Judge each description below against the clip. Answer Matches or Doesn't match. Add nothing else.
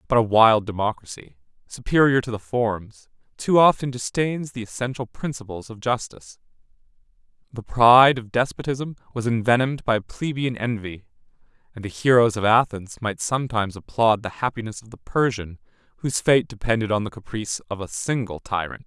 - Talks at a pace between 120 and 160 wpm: Matches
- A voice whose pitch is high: Doesn't match